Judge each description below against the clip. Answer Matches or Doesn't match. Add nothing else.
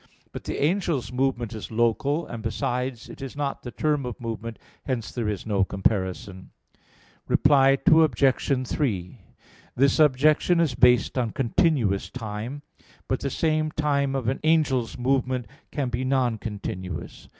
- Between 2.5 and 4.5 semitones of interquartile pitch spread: Matches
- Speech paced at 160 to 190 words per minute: Doesn't match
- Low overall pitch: Matches